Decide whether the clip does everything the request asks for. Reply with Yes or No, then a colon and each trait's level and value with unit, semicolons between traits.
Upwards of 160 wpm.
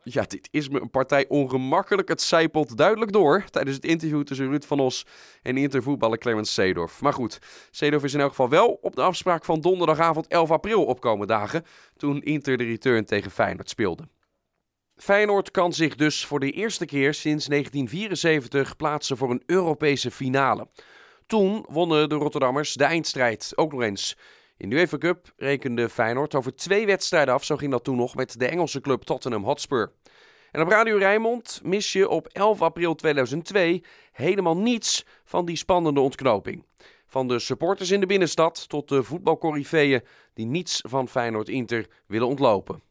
Yes: average, 170 wpm